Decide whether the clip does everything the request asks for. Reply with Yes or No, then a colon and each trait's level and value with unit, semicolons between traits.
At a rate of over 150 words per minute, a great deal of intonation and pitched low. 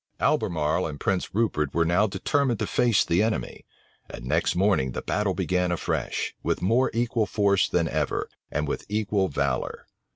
No: average, 165 wpm; average, 5.0 semitones; very low, 95 Hz